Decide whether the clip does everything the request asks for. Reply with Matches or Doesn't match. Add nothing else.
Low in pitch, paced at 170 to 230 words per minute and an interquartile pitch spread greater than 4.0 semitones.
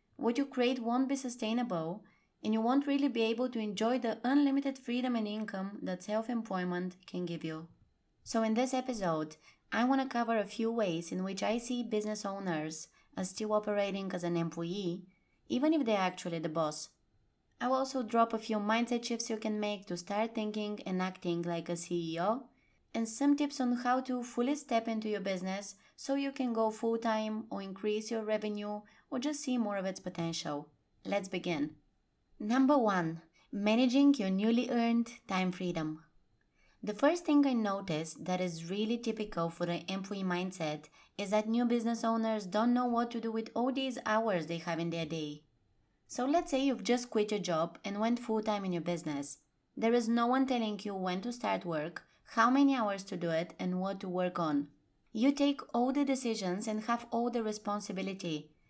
Doesn't match